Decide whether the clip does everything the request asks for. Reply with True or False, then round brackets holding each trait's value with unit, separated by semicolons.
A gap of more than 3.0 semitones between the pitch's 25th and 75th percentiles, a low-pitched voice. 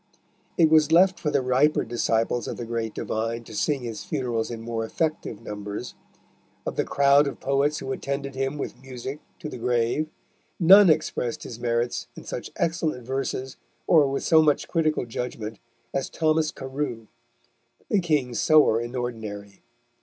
True (4.6 semitones; 130 Hz)